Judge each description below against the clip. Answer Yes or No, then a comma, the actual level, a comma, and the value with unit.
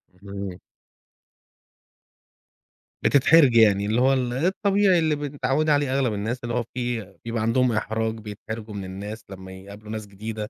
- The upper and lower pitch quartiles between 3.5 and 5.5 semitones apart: Yes, average, 4.3 semitones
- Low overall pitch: Yes, low, 115 Hz